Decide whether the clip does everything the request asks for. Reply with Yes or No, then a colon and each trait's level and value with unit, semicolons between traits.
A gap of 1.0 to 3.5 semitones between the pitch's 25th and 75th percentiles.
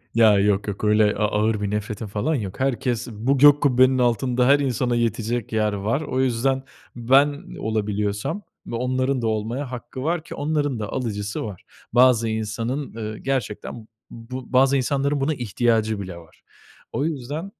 No: average, 3.9 semitones